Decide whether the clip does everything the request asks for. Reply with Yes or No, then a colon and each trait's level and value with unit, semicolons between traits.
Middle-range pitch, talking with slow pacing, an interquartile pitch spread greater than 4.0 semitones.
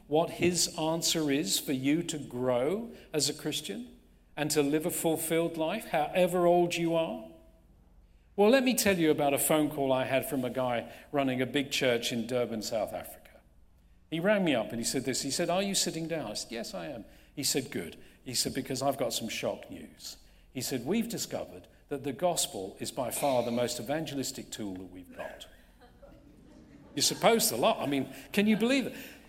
No: medium, 150 Hz; fast, 205 wpm; average, 5.0 semitones